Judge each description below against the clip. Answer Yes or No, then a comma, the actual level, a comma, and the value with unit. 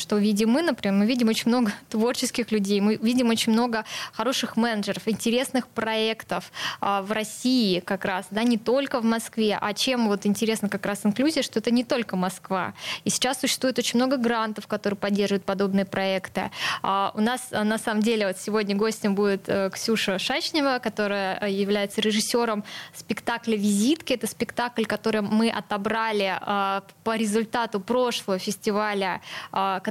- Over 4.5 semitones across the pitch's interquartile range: No, average, 2.7 semitones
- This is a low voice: No, high, 220 Hz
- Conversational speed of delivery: Yes, average, 150 wpm